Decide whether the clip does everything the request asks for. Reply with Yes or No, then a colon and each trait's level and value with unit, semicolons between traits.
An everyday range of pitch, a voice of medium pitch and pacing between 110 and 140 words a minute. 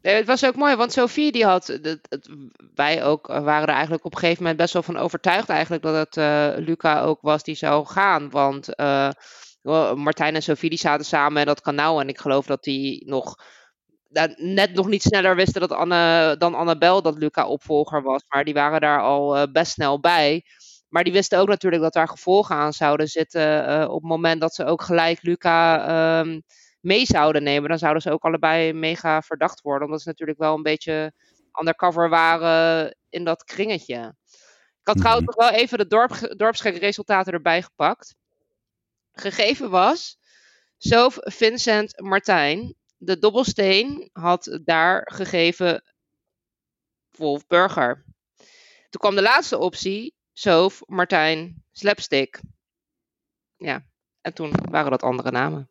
No: average, 4.0 semitones; medium, 165 Hz; average, 165 wpm